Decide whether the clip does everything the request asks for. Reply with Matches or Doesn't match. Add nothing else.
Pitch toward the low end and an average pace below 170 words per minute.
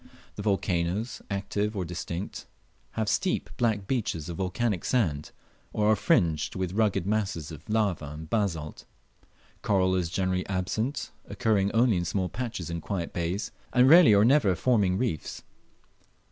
Matches